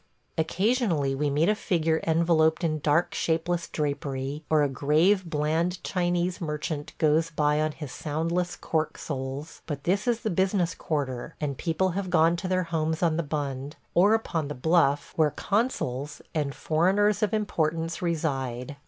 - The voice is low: No, medium, 160 Hz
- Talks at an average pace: Yes, average, 160 wpm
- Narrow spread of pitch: No, average, 3.1 semitones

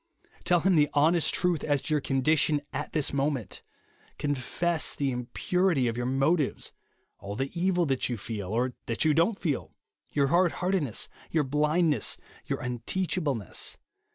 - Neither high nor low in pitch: Yes, medium, 145 Hz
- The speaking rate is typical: Yes, average, 155 wpm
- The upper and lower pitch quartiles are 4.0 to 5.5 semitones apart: Yes, average, 4.7 semitones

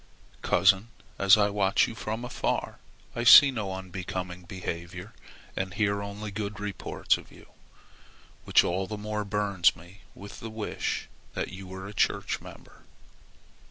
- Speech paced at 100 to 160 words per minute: Yes, average, 150 wpm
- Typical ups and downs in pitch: No, narrow, 2.0 semitones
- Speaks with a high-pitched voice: No, low, 100 Hz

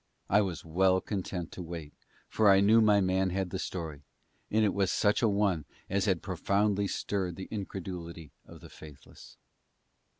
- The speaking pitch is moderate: No, very low, 95 Hz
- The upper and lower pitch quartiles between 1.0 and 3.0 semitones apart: Yes, narrow, 2.6 semitones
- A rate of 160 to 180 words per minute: Yes, average, 170 wpm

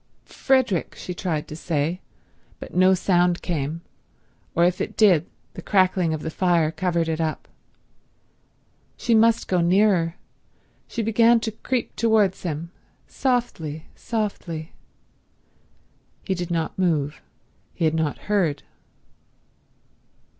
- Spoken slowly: Yes, slow, 120 wpm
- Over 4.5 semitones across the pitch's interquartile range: No, average, 4.2 semitones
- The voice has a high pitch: No, medium, 175 Hz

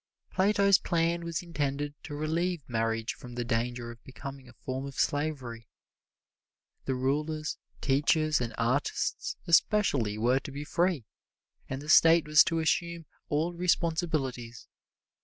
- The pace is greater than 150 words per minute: No, slow, 135 wpm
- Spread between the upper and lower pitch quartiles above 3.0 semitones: Yes, average, 4.8 semitones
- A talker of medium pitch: Yes, medium, 145 Hz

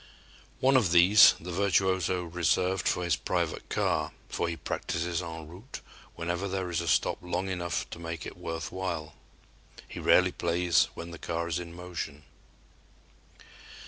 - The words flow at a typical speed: Yes, average, 155 wpm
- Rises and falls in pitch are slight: Yes, narrow, 1.7 semitones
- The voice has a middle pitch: No, very low, 85 Hz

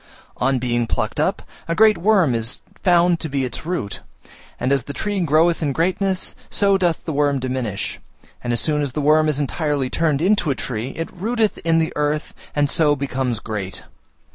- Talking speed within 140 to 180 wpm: No, average, 190 wpm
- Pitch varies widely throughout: No, average, 4.7 semitones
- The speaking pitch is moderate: Yes, medium, 150 Hz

